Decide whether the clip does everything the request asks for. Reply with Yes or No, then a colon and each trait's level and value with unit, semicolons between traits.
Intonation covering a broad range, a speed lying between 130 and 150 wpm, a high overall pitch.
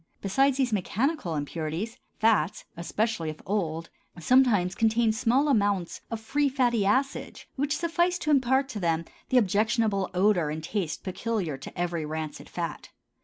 Yes: wide, 6.9 semitones; average, 145 wpm; high, 215 Hz